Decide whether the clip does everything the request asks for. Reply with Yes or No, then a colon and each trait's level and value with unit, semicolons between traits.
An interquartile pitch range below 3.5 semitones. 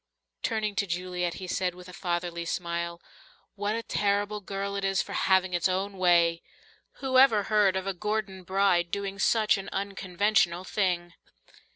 Yes: narrow, 2.4 semitones